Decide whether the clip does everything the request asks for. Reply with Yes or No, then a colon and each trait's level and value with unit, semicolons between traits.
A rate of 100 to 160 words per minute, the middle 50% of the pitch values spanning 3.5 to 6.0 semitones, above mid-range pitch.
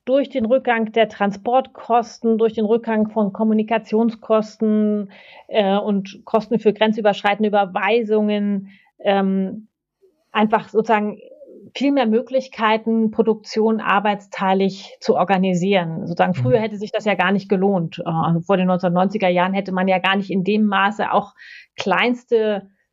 No: average, 130 wpm; narrow, 2.5 semitones; high, 210 Hz